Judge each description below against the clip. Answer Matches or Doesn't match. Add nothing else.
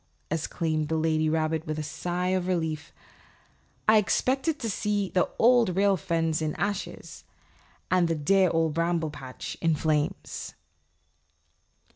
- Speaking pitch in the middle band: Matches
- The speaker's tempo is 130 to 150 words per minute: Matches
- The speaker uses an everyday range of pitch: Matches